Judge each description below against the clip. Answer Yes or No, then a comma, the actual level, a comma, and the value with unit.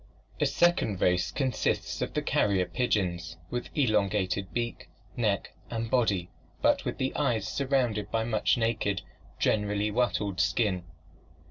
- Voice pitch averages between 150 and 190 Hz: No, low, 105 Hz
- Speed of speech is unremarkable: No, slow, 130 wpm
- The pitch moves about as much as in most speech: Yes, average, 3.9 semitones